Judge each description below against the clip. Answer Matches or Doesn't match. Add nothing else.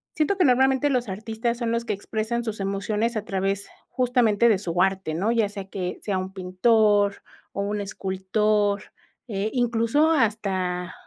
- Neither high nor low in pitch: Doesn't match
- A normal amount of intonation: Matches